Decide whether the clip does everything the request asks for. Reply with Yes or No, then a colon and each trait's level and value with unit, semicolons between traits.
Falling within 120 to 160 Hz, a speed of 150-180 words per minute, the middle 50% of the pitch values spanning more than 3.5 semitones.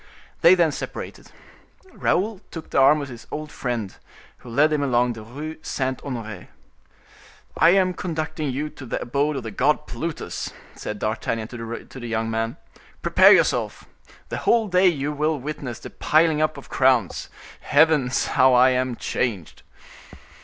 Yes: low, 135 Hz; average, 160 wpm; average, 4.6 semitones